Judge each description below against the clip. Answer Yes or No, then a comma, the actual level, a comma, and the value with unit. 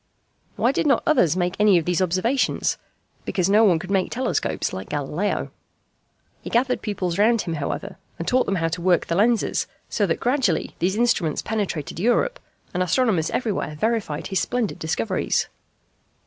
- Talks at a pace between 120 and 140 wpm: No, average, 165 wpm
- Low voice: No, high, 195 Hz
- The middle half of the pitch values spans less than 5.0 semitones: No, wide, 5.5 semitones